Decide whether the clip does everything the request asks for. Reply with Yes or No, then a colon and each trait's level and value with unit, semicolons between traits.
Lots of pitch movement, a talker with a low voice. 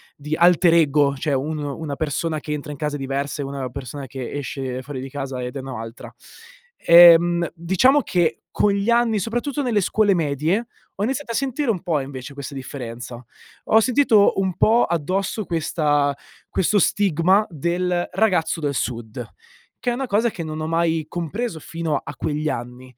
No: wide, 5.7 semitones; medium, 160 Hz